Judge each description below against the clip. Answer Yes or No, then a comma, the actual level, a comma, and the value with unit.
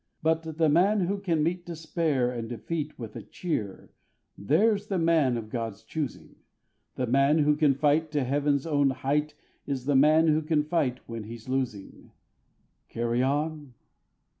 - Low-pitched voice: No, medium, 145 Hz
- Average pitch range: Yes, average, 4.1 semitones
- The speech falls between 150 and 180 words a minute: Yes, average, 160 wpm